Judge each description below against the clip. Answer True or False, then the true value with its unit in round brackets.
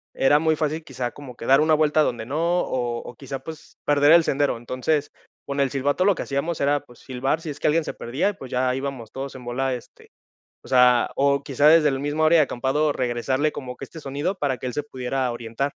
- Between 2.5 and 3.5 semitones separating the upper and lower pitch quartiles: True (2.9 semitones)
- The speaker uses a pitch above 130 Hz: True (140 Hz)